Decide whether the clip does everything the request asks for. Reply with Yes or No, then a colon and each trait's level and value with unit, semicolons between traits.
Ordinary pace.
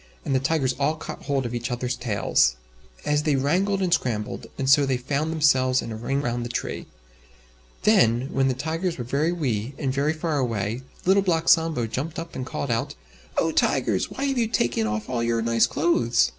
No: fast, 210 wpm